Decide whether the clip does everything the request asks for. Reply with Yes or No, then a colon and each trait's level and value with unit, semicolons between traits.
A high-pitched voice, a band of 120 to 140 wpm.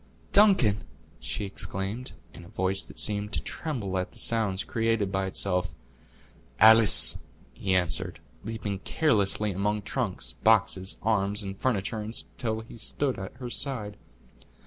No: low, 105 Hz; slow, 135 wpm